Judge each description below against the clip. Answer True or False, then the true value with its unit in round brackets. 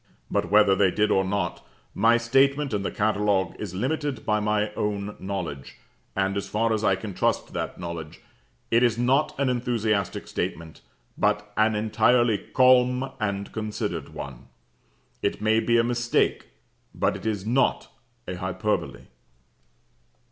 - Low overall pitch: True (105 Hz)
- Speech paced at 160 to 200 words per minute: False (150 wpm)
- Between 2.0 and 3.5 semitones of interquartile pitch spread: True (3.2 semitones)